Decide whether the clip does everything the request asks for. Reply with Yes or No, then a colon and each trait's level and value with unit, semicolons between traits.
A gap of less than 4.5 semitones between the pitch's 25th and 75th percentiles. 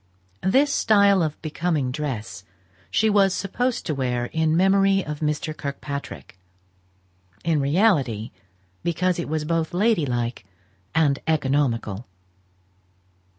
No: wide, 5.6 semitones